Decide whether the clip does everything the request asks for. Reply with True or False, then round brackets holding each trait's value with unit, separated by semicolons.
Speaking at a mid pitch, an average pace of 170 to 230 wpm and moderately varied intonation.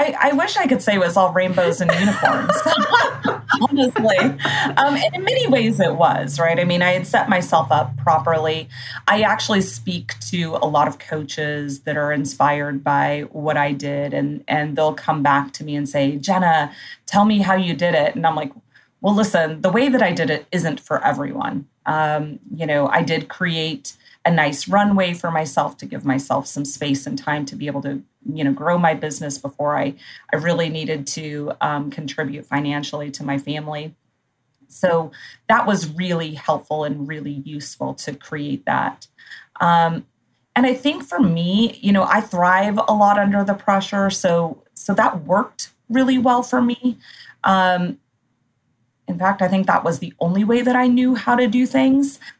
False (165 Hz; 190 wpm; 5.7 semitones)